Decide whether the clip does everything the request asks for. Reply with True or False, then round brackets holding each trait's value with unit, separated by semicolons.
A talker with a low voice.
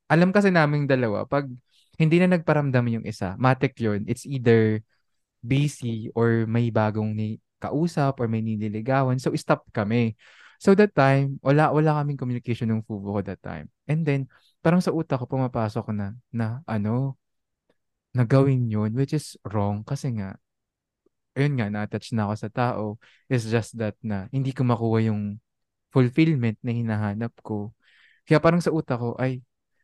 True (120 Hz)